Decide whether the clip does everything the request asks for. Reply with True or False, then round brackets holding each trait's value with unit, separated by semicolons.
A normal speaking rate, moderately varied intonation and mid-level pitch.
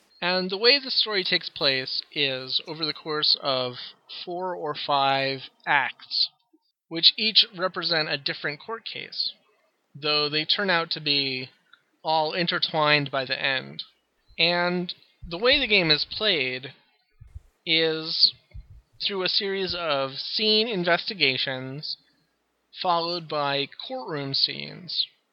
False (125 wpm; 4.5 semitones; 160 Hz)